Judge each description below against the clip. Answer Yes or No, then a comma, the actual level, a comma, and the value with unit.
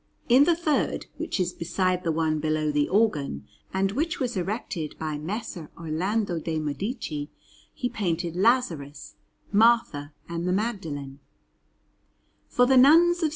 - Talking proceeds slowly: No, average, 145 wpm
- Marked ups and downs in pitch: Yes, wide, 7.0 semitones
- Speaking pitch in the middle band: Yes, medium, 180 Hz